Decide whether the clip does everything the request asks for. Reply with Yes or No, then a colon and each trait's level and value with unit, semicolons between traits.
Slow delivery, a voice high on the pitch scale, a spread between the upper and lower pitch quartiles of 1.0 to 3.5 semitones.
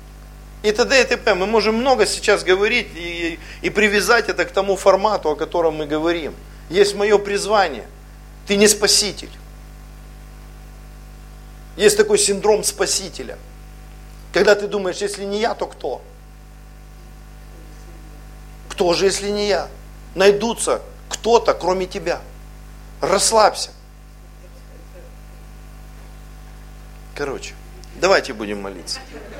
Yes: slow, 105 wpm; high, 200 Hz; average, 2.9 semitones